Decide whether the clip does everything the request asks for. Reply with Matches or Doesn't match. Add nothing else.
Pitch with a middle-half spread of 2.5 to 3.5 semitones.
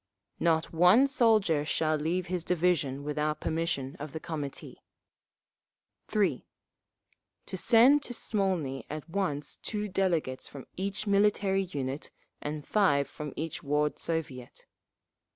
Doesn't match